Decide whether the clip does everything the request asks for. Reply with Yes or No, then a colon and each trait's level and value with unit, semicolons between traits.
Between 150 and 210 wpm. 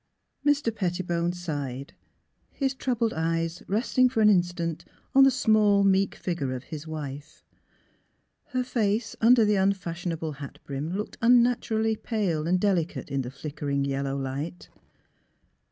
No: slow, 135 wpm